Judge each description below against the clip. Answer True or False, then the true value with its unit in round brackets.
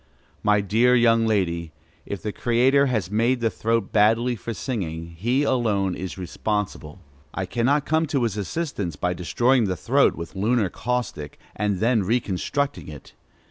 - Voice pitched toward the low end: True (110 Hz)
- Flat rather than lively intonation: False (4.7 semitones)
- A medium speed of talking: True (155 wpm)